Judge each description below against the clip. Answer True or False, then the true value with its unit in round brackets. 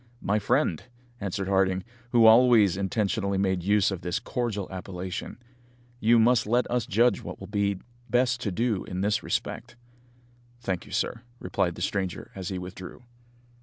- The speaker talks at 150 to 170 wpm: True (165 wpm)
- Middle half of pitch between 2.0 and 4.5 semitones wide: True (3.6 semitones)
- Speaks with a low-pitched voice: True (100 Hz)